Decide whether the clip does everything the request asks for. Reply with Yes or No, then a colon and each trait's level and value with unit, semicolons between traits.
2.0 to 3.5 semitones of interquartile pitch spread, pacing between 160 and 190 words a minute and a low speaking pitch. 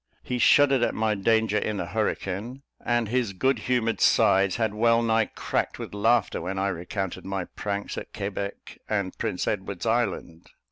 Yes: average, 3.1 semitones; average, 170 wpm; low, 105 Hz